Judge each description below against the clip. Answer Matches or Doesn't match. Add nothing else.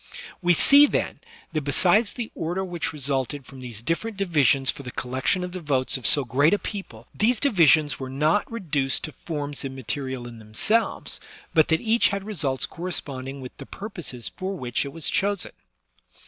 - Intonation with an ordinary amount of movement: Doesn't match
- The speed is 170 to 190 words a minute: Matches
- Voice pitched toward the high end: Doesn't match